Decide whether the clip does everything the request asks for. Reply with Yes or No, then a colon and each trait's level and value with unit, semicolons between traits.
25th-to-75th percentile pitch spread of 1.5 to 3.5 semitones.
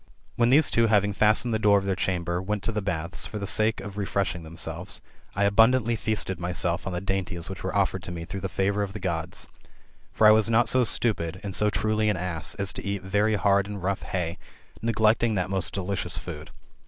Yes: average, 2.8 semitones